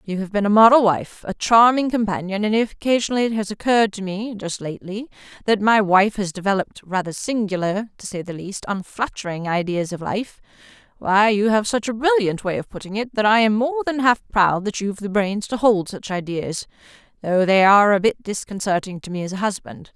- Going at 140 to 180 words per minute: No, average, 200 wpm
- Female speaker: Yes, female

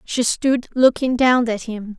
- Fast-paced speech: No, average, 180 wpm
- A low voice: No, high, 240 Hz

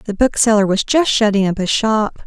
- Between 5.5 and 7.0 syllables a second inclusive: No, 4.9 syllables/s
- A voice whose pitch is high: Yes, high, 215 Hz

